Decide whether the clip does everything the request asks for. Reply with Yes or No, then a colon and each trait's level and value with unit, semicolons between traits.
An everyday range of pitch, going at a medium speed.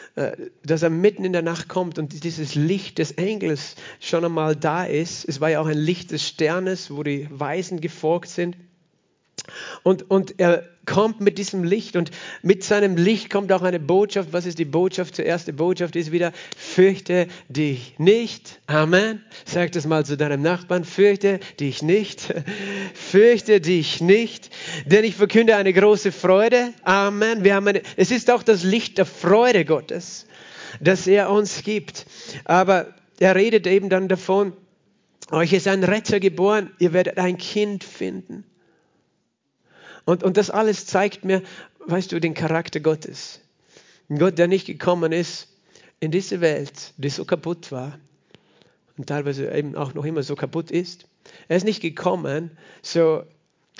Yes: average, 3.3 semitones; average, 165 wpm